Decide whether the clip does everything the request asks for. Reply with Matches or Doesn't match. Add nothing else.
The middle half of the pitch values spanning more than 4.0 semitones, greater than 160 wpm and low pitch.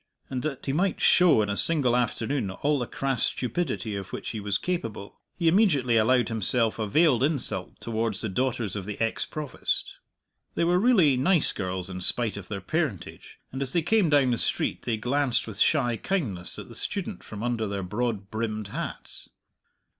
Matches